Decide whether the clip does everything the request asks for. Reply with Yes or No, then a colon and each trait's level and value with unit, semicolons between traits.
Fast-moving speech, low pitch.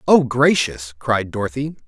No: slow, 130 wpm; low, 125 Hz